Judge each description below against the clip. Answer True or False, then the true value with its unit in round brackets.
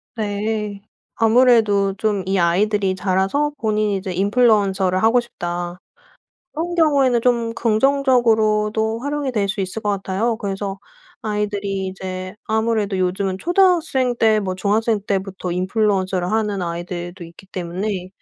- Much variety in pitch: False (2.9 semitones)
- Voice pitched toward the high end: True (205 Hz)